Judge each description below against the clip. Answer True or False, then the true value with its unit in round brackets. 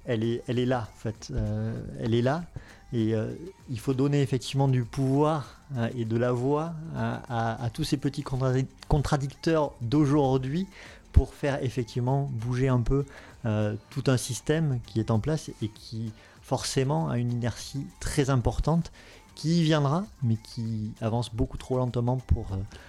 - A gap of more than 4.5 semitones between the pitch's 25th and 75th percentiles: False (3.7 semitones)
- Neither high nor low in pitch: False (125 Hz)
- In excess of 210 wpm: False (175 wpm)